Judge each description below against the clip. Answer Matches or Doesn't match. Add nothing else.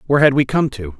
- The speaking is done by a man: Matches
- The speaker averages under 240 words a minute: Doesn't match